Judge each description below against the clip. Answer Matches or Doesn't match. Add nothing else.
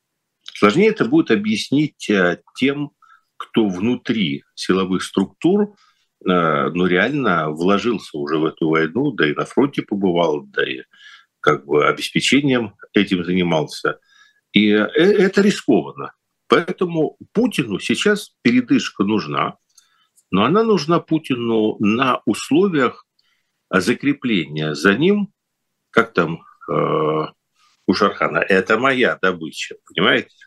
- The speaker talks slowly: Matches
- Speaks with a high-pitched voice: Doesn't match